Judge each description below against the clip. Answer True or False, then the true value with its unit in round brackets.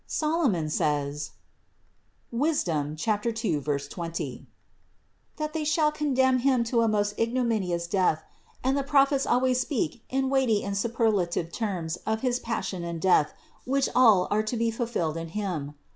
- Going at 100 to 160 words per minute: True (150 wpm)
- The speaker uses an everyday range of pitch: False (7.2 semitones)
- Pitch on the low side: False (220 Hz)